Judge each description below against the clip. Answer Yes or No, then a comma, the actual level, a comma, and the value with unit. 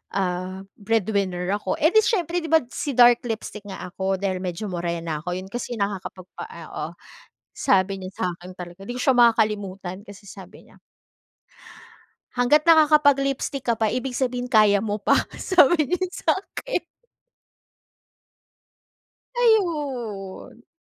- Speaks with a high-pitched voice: Yes, high, 215 Hz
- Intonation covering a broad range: Yes, wide, 6.4 semitones